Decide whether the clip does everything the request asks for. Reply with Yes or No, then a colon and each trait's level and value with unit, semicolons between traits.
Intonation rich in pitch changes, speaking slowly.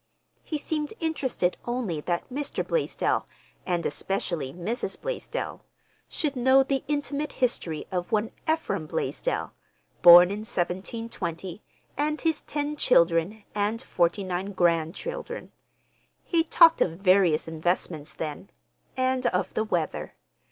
Yes: wide, 8.3 semitones; slow, 120 wpm